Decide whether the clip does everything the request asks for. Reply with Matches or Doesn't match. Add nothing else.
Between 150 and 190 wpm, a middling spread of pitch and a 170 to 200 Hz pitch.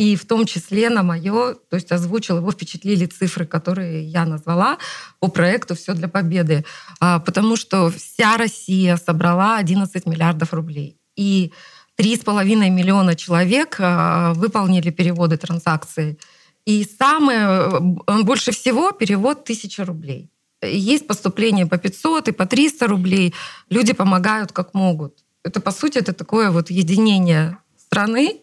Doesn't match